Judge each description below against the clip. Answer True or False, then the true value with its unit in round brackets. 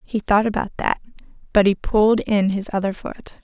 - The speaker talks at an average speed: True (190 wpm)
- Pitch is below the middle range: False (205 Hz)